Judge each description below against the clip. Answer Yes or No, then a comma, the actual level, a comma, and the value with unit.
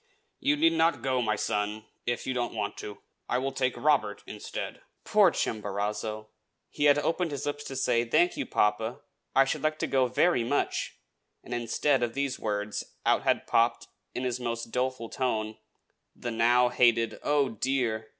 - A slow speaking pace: No, average, 180 wpm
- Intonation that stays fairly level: No, average, 3.6 semitones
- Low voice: Yes, low, 125 Hz